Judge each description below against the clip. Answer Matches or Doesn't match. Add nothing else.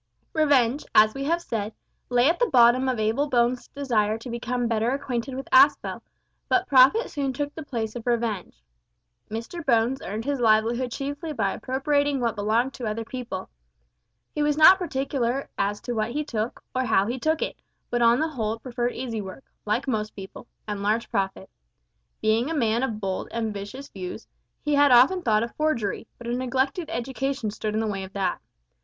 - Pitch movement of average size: Matches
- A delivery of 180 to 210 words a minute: Matches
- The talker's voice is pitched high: Matches